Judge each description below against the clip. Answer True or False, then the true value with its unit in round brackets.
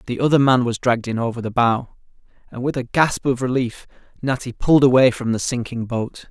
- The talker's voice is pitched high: False (125 Hz)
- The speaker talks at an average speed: False (210 wpm)